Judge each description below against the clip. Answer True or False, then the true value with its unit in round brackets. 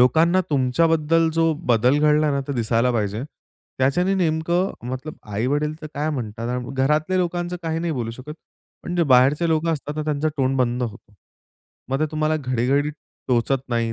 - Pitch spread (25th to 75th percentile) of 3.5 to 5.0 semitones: True (4.2 semitones)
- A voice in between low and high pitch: True (145 Hz)